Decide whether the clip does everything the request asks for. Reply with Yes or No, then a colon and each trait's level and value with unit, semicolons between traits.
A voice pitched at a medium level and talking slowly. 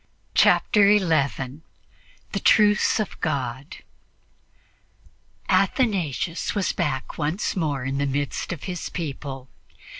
Yes: medium, 155 Hz; slow, 100 wpm